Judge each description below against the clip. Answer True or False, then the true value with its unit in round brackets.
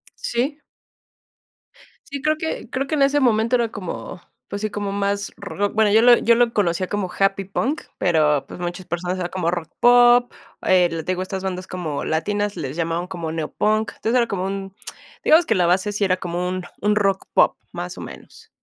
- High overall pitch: True (195 Hz)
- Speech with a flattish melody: False (3.9 semitones)